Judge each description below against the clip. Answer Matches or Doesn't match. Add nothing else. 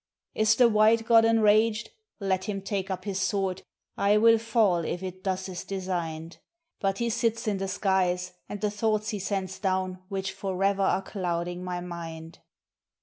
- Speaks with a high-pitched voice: Matches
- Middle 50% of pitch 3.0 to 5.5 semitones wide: Doesn't match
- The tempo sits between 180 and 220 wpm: Doesn't match